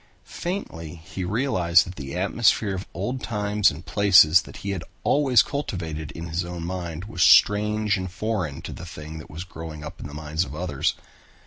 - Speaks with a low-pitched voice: Yes, very low, 90 Hz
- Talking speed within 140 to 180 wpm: No, average, 190 wpm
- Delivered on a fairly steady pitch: No, average, 4.4 semitones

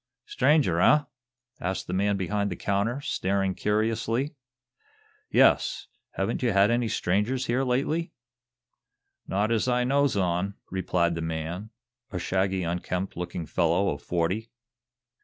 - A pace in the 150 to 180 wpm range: No, slow, 135 wpm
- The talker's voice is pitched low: Yes, low, 100 Hz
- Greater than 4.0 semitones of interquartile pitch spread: Yes, average, 4.8 semitones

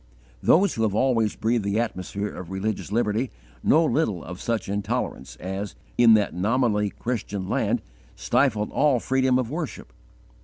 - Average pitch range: Yes, average, 4.0 semitones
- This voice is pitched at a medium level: No, low, 110 Hz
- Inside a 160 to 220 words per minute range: No, average, 150 wpm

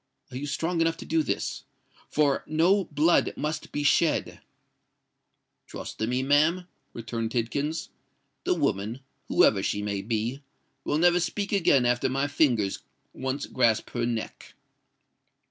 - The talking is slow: Yes, slow, 130 wpm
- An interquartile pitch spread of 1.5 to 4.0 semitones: No, average, 5.2 semitones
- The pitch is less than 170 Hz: Yes, medium, 140 Hz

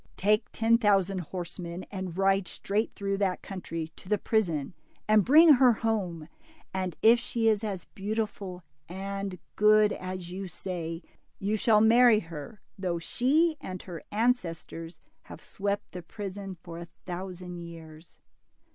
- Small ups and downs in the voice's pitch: No, average, 3.4 semitones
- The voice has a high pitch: Yes, high, 195 Hz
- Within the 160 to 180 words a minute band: No, average, 145 wpm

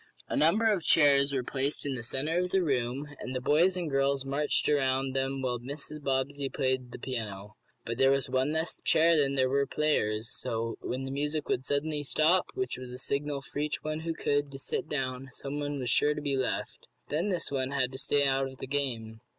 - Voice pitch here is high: No, medium, 140 Hz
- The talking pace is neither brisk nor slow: No, fast, 225 wpm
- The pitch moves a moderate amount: No, narrow, 2.3 semitones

